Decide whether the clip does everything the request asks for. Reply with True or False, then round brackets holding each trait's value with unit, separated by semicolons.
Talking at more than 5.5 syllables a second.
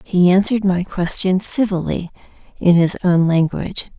False (4.9 syllables/s)